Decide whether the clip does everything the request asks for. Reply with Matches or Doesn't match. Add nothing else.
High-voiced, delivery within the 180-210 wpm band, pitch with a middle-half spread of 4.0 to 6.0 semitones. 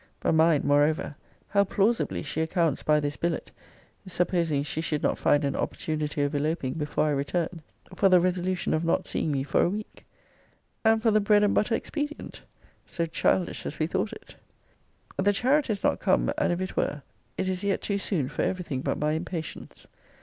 Doesn't match